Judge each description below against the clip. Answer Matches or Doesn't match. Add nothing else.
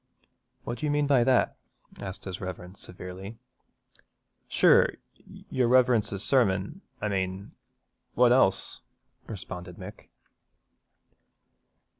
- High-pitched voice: Doesn't match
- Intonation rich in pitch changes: Doesn't match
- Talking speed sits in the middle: Doesn't match